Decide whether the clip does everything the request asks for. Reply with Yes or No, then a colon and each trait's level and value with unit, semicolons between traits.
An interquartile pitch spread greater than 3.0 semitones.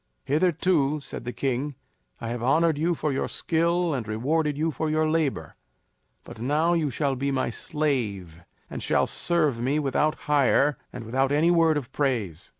Yes: average, 3.9 semitones